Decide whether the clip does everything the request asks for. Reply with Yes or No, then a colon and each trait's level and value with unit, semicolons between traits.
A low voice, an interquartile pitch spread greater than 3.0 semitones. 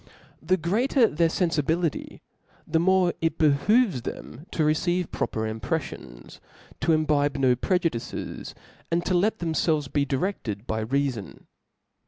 No: medium, 155 Hz; average, 4.6 semitones